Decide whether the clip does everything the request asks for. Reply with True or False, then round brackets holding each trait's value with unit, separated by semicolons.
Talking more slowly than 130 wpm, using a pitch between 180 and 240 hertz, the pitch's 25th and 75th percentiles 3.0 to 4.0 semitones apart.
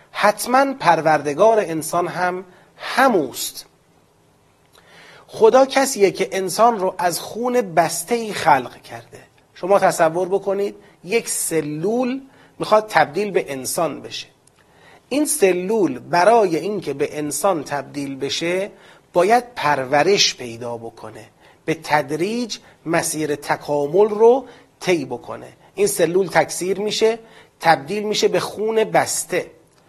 False (110 wpm; 190 Hz; 5.5 semitones)